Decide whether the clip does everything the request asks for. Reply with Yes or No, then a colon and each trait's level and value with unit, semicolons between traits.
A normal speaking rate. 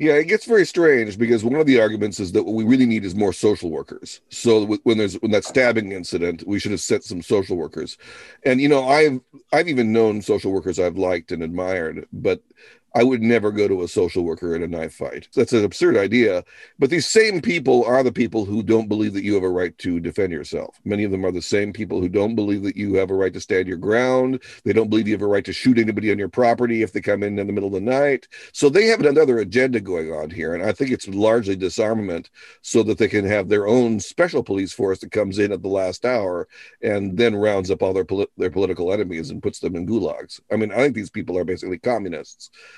No: fast, 250 wpm